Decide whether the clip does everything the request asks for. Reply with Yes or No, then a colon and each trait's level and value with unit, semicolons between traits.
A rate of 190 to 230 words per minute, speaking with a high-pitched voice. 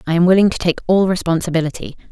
No: average, 200 wpm; medium, 175 Hz